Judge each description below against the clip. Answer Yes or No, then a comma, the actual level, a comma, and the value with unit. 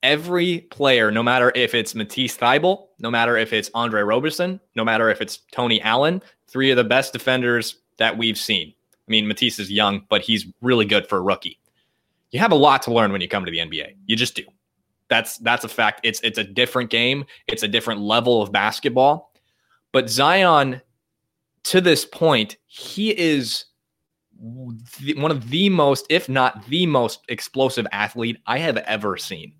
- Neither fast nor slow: Yes, average, 185 wpm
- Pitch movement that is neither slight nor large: Yes, average, 3.4 semitones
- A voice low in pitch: Yes, low, 120 Hz